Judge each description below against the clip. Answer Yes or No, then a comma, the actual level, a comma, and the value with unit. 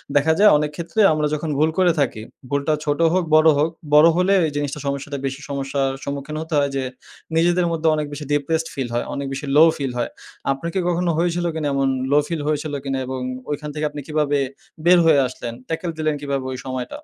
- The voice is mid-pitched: Yes, medium, 150 Hz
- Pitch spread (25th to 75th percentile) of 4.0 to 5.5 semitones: No, average, 2.7 semitones